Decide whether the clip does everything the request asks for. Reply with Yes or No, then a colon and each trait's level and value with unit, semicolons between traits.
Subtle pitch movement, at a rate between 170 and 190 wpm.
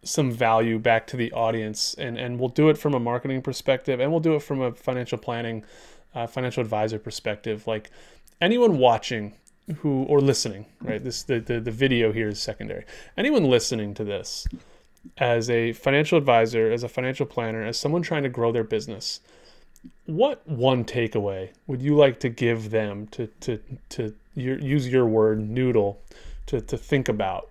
No: average, 3.1 semitones; average, 180 wpm